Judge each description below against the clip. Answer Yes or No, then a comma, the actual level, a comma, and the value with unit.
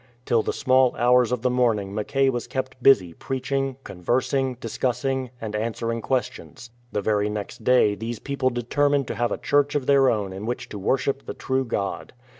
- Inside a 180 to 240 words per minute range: Yes, average, 195 wpm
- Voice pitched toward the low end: Yes, low, 125 Hz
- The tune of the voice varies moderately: Yes, average, 3.3 semitones